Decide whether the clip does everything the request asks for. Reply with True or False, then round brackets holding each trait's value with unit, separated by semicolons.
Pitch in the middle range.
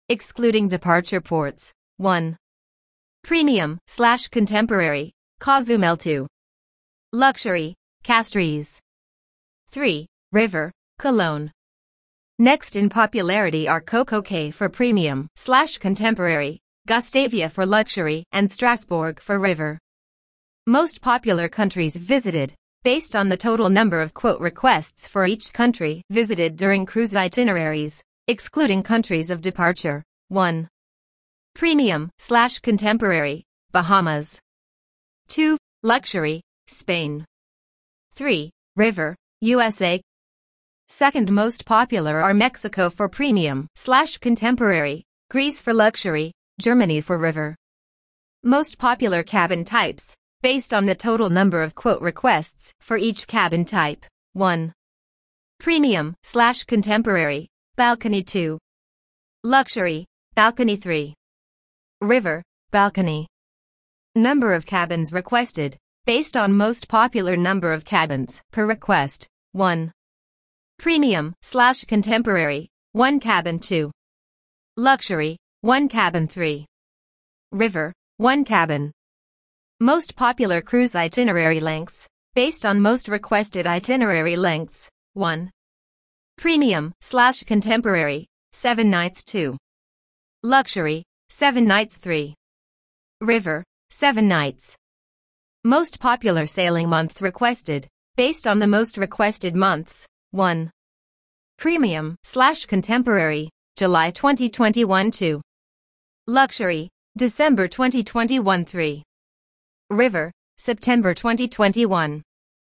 False (200 Hz)